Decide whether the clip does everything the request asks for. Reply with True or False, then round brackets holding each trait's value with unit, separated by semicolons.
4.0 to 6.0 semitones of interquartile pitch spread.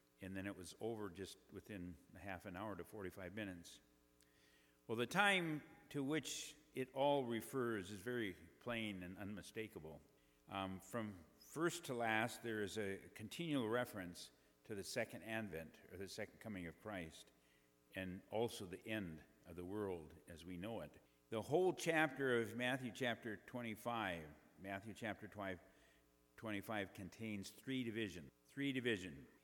True (5.0 semitones)